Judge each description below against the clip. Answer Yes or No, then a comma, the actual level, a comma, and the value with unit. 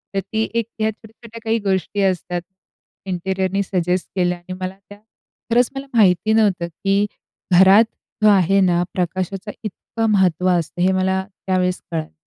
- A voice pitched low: No, high, 190 Hz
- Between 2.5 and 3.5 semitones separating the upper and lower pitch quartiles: Yes, average, 2.8 semitones